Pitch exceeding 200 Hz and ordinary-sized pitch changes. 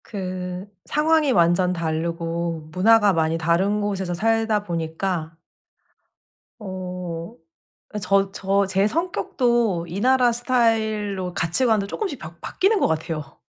No: high, 190 Hz; average, 4.8 semitones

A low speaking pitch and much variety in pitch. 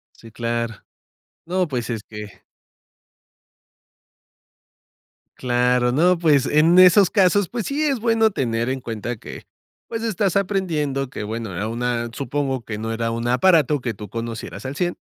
Yes: low, 130 Hz; wide, 7.5 semitones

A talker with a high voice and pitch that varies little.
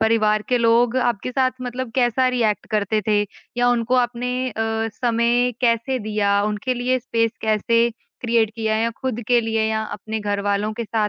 Yes: high, 230 Hz; narrow, 2.1 semitones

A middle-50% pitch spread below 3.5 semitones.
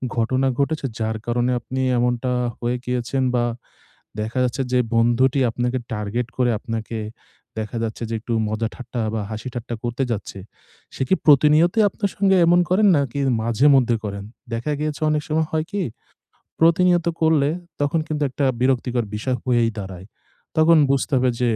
No: average, 4.3 semitones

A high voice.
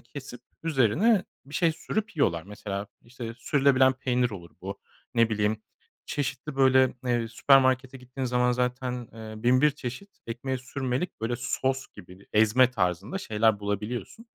No: low, 125 Hz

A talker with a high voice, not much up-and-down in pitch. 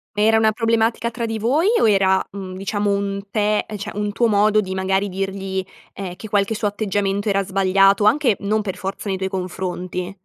Yes: high, 200 Hz; narrow, 1.9 semitones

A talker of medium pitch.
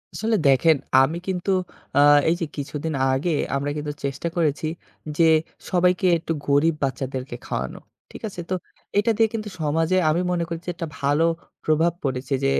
Yes: medium, 160 Hz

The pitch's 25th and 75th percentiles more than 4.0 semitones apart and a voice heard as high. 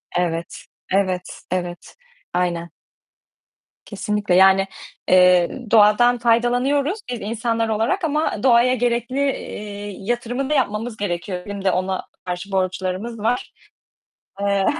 Yes: average, 4.4 semitones; high, 205 Hz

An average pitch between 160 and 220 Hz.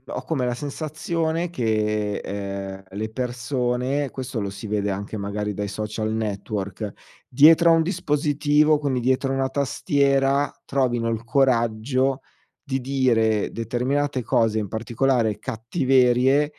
No: low, 125 Hz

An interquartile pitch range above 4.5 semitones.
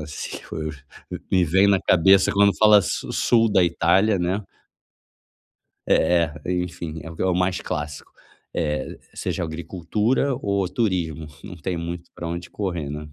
No: average, 3.2 semitones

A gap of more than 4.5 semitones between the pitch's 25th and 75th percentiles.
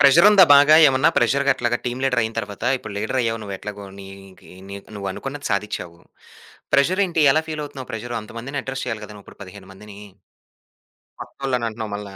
Yes: average, 5.2 semitones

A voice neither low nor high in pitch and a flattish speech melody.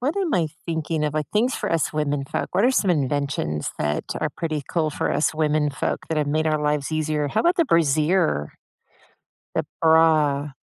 Yes: medium, 155 Hz; narrow, 2.2 semitones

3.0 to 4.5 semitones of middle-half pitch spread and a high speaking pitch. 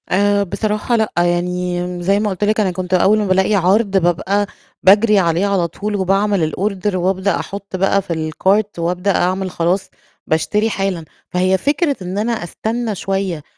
No: narrow, 2.5 semitones; high, 195 Hz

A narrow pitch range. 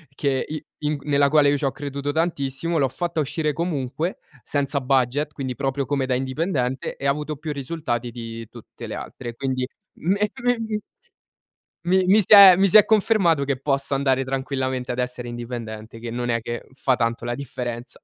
No: average, 3.6 semitones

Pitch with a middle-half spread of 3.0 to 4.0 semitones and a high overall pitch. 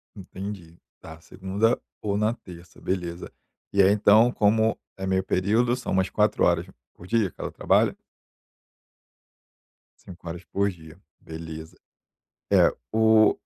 No: average, 3.7 semitones; very low, 95 Hz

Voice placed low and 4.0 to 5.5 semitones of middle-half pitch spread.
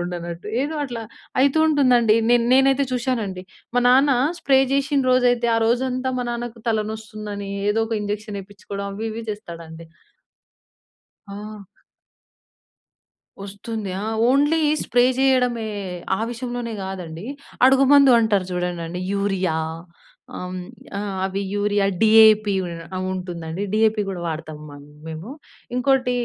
No: high, 220 Hz; average, 4.3 semitones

